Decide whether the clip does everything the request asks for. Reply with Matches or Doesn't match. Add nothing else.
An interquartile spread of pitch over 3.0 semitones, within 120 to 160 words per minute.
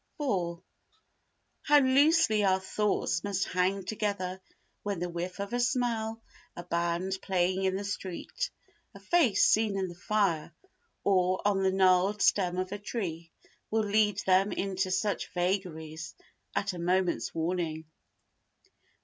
Doesn't match